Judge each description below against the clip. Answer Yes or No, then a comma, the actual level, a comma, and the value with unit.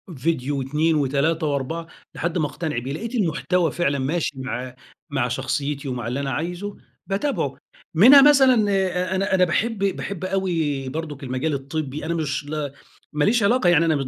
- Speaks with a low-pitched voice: No, medium, 155 Hz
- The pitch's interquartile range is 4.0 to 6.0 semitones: Yes, average, 4.7 semitones